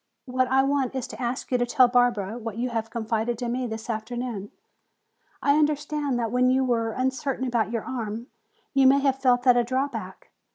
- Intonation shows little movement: Yes, narrow, 2.3 semitones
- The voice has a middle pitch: No, high, 245 Hz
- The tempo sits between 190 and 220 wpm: Yes, average, 200 wpm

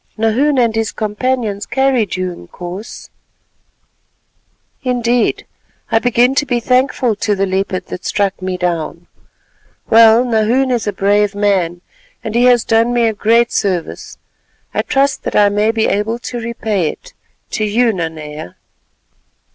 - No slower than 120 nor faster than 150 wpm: Yes, average, 140 wpm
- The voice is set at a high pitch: Yes, high, 220 Hz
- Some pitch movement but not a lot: Yes, average, 3.6 semitones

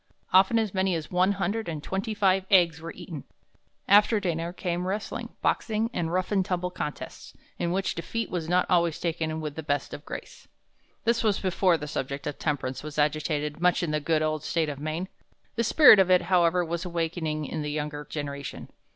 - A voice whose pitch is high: No, medium, 170 Hz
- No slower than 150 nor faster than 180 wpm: No, average, 195 wpm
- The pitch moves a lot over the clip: No, average, 3.5 semitones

